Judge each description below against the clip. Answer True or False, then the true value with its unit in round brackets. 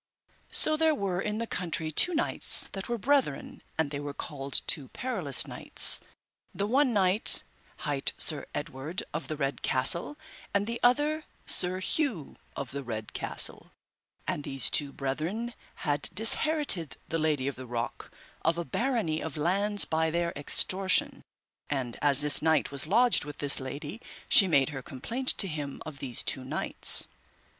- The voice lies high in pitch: False (160 Hz)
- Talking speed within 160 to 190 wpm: True (165 wpm)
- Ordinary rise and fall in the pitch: False (7.0 semitones)